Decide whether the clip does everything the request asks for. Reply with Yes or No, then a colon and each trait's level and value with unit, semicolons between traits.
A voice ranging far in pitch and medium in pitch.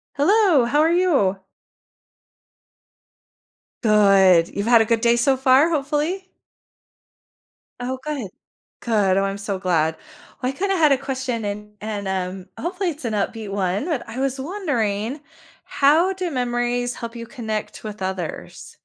No: wide, 6.1 semitones; high, 240 Hz